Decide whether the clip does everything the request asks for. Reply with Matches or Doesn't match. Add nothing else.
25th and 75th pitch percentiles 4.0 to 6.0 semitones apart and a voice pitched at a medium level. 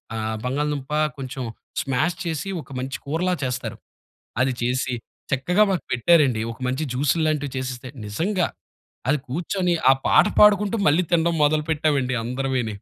Matches